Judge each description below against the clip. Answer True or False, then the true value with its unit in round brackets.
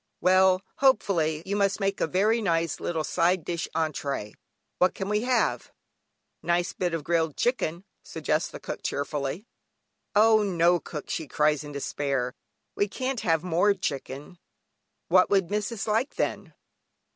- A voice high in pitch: False (175 Hz)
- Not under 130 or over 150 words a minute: True (145 wpm)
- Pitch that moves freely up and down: False (4.4 semitones)